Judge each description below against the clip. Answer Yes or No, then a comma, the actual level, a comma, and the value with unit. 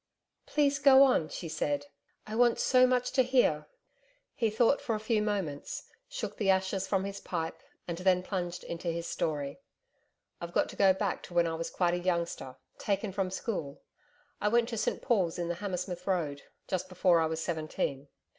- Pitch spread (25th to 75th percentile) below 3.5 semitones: No, average, 4.3 semitones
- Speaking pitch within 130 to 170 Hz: No, medium, 185 Hz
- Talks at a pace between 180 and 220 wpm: Yes, average, 190 wpm